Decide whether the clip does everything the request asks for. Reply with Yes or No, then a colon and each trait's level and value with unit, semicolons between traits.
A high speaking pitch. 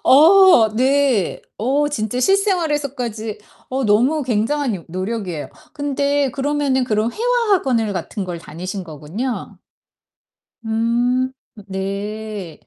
Yes: high, 240 Hz